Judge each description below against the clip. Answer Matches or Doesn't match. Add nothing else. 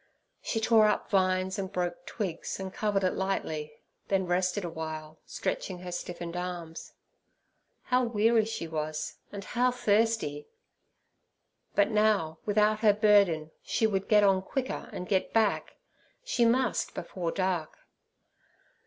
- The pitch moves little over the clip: Doesn't match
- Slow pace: Matches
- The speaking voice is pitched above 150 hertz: Matches